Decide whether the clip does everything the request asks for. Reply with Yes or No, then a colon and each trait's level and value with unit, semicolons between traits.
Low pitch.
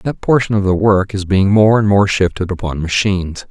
Yes: low, 100 Hz